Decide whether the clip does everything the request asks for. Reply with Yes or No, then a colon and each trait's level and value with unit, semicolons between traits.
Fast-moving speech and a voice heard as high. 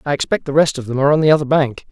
No: fast, 345 wpm; medium, 145 Hz